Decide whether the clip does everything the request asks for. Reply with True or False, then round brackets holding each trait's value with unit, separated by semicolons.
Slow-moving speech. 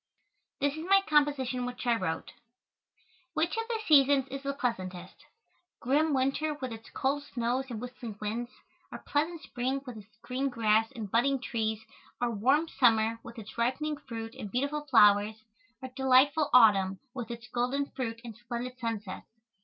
False (160 wpm)